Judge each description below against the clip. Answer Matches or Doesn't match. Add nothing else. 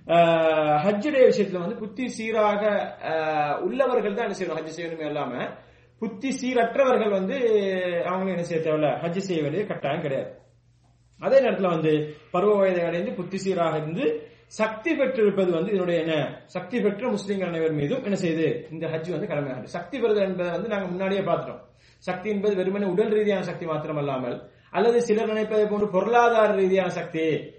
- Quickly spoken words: Doesn't match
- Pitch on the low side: Doesn't match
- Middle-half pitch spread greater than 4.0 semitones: Matches